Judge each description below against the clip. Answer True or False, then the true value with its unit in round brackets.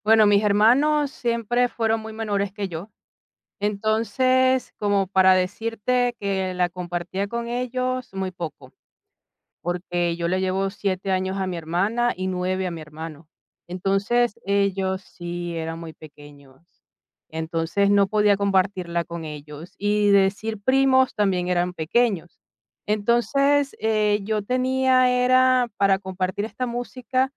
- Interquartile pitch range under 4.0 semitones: False (4.6 semitones)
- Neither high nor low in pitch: False (200 Hz)